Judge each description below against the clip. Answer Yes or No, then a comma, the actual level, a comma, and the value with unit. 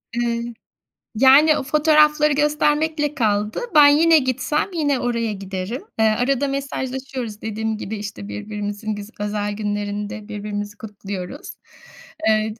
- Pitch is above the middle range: Yes, high, 220 Hz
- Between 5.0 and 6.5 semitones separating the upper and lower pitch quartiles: Yes, wide, 5.6 semitones